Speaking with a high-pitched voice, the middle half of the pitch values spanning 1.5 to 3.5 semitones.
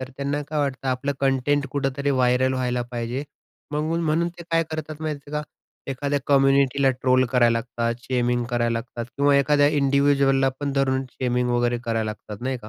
No: low, 135 Hz; narrow, 2.4 semitones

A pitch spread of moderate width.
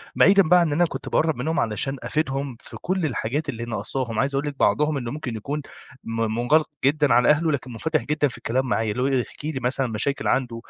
Yes: average, 4.0 semitones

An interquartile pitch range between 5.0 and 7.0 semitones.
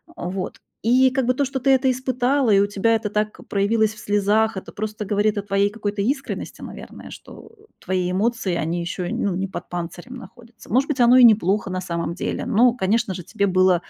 No: average, 4.3 semitones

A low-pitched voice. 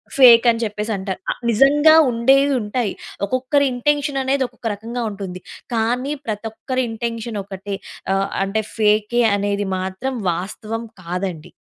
No: high, 225 Hz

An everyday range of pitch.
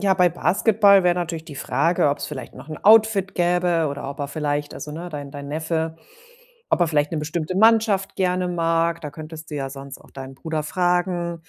Yes: average, 3.4 semitones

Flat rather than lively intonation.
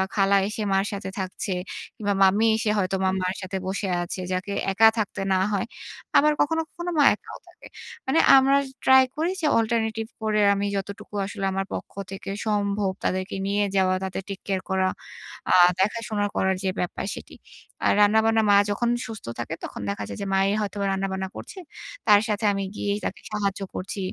Yes: narrow, 2.3 semitones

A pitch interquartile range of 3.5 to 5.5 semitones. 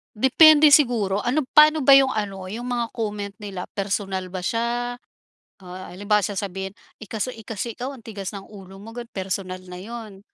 Yes: average, 3.9 semitones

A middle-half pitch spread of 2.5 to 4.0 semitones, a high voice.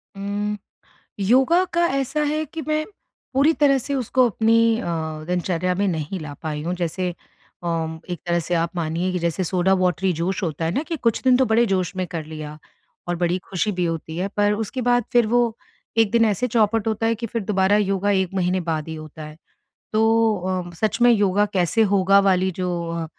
No: average, 4.6 semitones; high, 195 Hz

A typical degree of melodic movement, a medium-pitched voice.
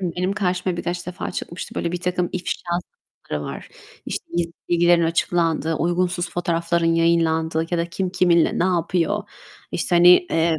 No: narrow, 1.3 semitones; medium, 170 Hz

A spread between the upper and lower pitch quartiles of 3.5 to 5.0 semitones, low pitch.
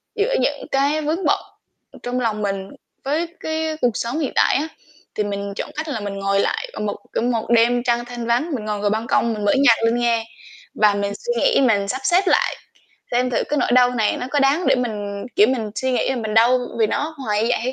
No: average, 4.3 semitones; high, 240 Hz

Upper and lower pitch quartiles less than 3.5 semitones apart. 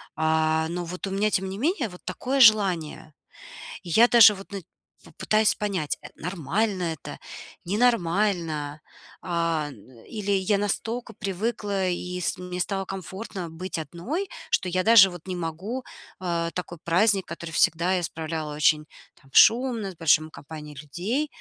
No: average, 4.2 semitones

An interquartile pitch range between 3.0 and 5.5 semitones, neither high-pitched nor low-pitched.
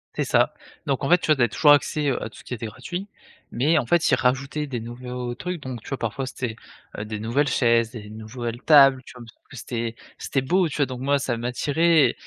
No: average, 3.6 semitones; low, 130 Hz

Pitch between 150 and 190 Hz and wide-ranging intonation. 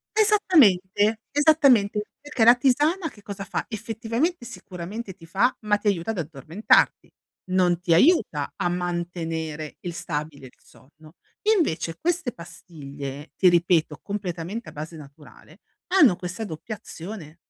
Yes: medium, 185 Hz; wide, 5.8 semitones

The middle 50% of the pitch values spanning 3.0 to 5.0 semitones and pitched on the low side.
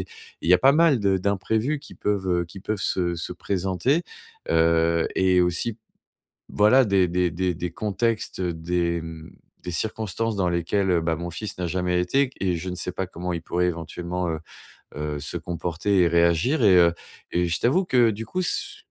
Yes: average, 3.4 semitones; very low, 90 Hz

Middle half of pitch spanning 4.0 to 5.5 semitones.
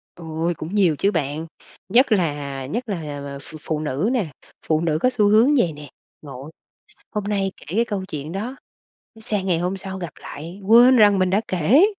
Yes: average, 5.2 semitones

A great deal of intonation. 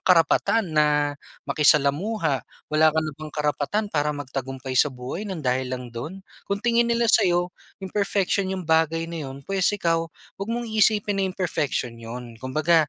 Yes: wide, 5.8 semitones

